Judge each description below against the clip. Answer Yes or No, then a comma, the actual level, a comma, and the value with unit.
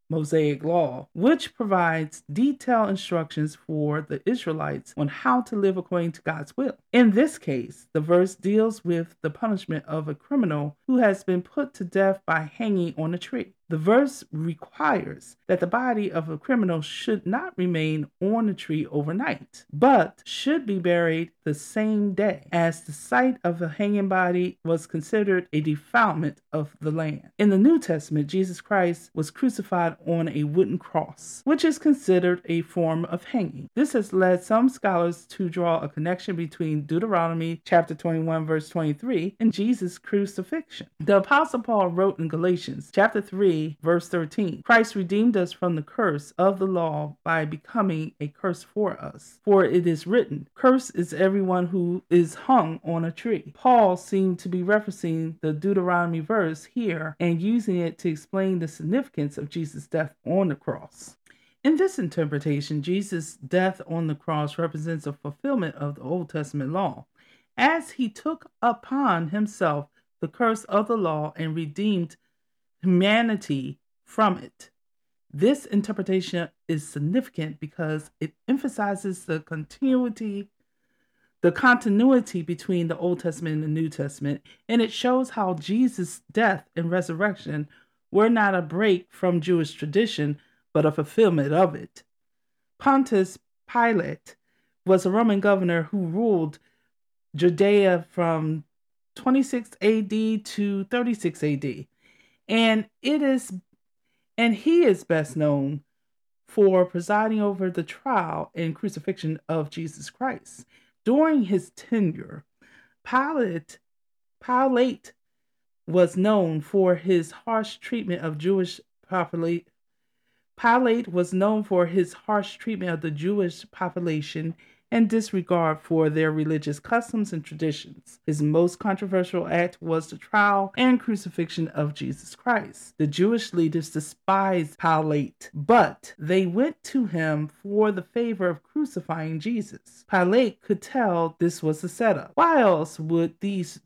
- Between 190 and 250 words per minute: No, average, 145 wpm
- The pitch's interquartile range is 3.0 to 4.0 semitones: No, average, 4.8 semitones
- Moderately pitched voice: Yes, medium, 180 Hz